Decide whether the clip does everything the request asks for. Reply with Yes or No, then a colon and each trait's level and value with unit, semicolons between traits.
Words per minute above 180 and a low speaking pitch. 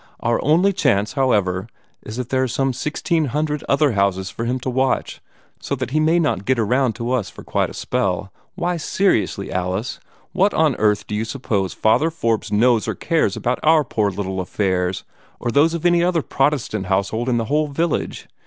Yes: average, 195 wpm; low, 125 Hz